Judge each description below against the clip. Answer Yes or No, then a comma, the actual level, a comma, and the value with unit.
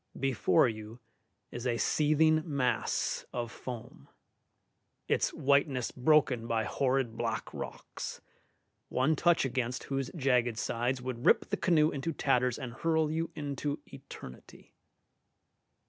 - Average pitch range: Yes, average, 3.6 semitones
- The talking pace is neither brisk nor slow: No, slow, 120 wpm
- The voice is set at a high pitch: No, low, 130 Hz